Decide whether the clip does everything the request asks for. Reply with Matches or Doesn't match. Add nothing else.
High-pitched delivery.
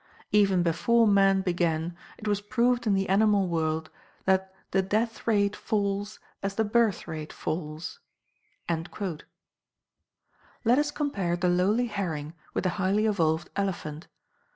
Matches